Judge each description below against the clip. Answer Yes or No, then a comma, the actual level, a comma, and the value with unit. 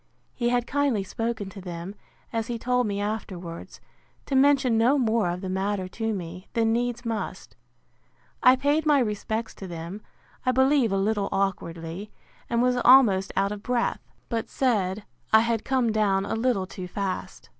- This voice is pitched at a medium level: No, high, 220 Hz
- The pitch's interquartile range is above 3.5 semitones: Yes, average, 4.0 semitones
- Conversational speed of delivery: Yes, average, 170 wpm